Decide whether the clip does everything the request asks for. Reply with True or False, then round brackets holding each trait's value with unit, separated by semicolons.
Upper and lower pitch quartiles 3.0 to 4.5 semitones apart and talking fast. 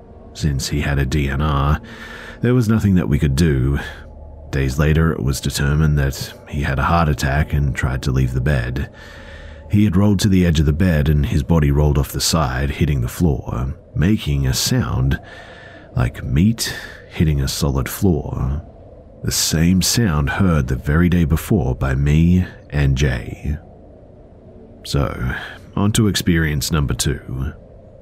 False (3.9 semitones; 160 wpm)